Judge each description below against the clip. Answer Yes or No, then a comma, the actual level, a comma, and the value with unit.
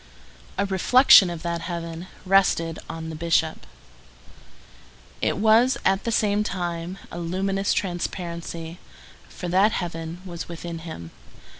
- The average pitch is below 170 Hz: No, medium, 175 Hz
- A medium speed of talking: No, slow, 125 wpm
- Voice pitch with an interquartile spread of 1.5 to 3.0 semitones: Yes, average, 2.7 semitones